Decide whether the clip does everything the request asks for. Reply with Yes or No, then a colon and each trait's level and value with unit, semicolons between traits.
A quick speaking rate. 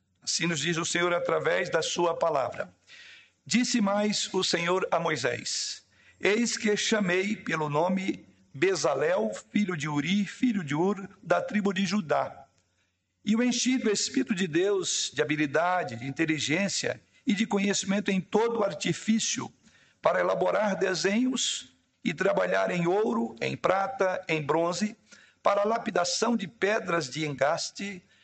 No: average, 140 wpm